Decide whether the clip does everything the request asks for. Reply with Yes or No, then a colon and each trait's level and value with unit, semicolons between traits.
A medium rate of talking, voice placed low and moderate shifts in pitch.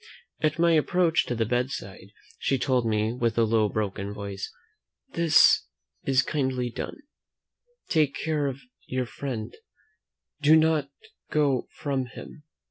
No: slow, 130 wpm; low, 130 Hz; average, 5.0 semitones